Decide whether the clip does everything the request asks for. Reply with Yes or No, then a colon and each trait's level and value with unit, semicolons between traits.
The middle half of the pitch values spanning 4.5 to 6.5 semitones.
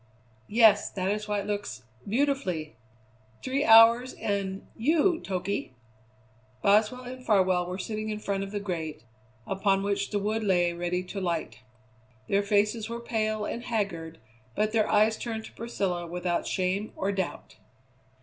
No: average, 3.1 semitones